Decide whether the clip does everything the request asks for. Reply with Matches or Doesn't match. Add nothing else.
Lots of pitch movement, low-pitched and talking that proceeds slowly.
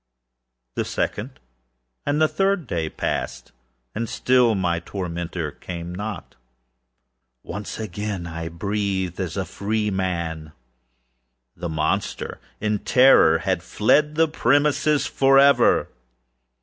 Matches